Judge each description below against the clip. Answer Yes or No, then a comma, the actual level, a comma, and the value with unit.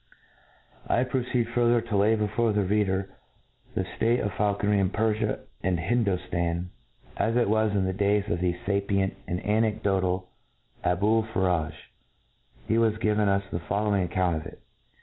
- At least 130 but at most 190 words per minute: Yes, average, 150 wpm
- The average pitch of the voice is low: Yes, low, 100 Hz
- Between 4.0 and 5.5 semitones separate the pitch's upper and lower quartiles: No, average, 2.8 semitones